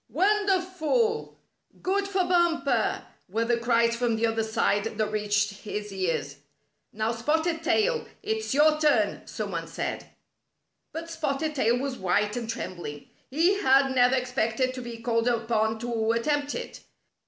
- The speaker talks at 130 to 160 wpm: Yes, average, 150 wpm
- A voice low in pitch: No, high, 245 Hz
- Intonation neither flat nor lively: No, wide, 6.4 semitones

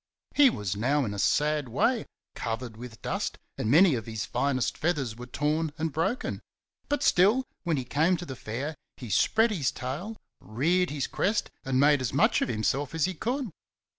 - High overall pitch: No, medium, 145 Hz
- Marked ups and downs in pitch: Yes, wide, 6.1 semitones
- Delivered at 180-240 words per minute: Yes, average, 190 wpm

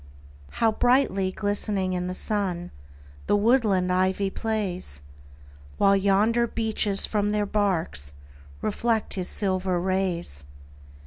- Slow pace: Yes, slow, 110 wpm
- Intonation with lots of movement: No, narrow, 2.6 semitones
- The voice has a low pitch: No, high, 195 Hz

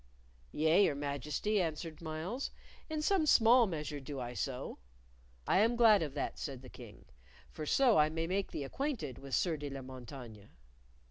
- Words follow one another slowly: No, average, 175 wpm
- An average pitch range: No, wide, 7.2 semitones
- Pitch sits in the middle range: Yes, medium, 155 Hz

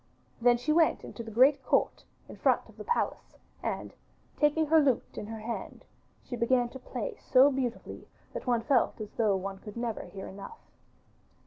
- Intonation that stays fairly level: No, average, 4.1 semitones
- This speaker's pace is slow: No, average, 185 wpm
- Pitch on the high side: Yes, high, 245 Hz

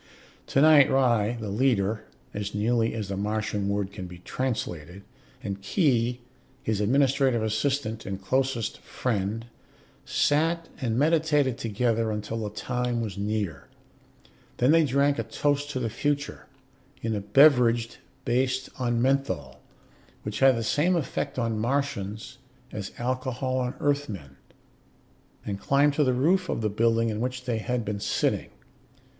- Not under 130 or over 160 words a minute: Yes, average, 140 wpm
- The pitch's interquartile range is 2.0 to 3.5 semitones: No, average, 4.3 semitones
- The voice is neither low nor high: No, low, 120 Hz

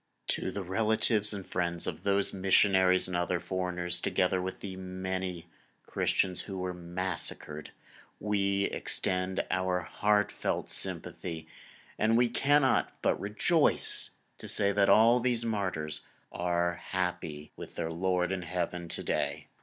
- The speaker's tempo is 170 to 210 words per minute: No, slow, 135 wpm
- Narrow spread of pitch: Yes, narrow, 2.3 semitones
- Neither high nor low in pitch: No, very low, 95 Hz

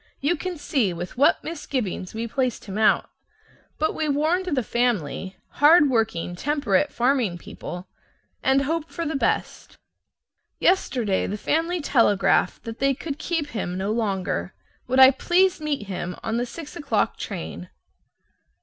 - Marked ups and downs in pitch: Yes, wide, 6.9 semitones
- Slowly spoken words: No, average, 150 wpm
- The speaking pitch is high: Yes, very high, 255 Hz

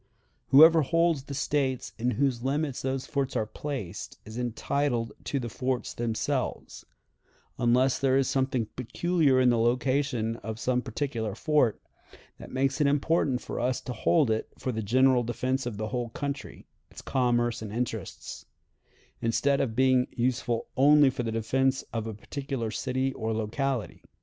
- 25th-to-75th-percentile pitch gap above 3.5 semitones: No, average, 2.9 semitones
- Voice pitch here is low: Yes, low, 130 Hz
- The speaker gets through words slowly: No, average, 160 wpm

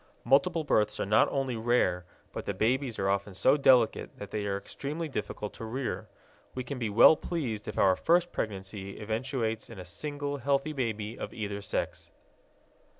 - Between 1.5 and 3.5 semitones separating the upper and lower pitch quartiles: No, average, 5.1 semitones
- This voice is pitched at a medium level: No, low, 115 Hz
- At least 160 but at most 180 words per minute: Yes, average, 175 wpm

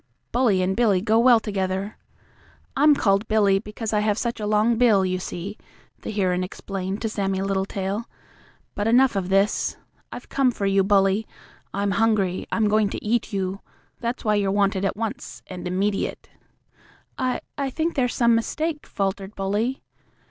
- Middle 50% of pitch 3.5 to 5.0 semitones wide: No, average, 2.8 semitones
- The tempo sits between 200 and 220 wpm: No, average, 165 wpm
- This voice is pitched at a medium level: No, high, 205 Hz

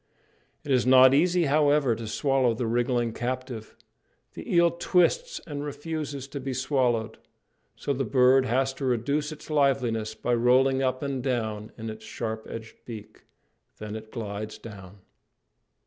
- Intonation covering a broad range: No, average, 3.8 semitones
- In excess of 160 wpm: No, average, 150 wpm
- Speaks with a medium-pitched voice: No, low, 130 Hz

